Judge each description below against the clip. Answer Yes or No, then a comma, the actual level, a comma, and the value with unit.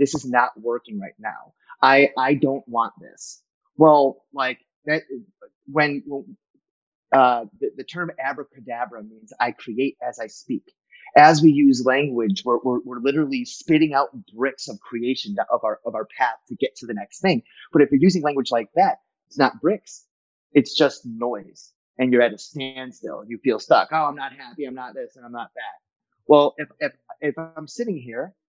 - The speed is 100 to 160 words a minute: No, average, 190 wpm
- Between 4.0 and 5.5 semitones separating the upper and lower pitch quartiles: Yes, average, 4.3 semitones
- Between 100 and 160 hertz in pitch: Yes, medium, 140 Hz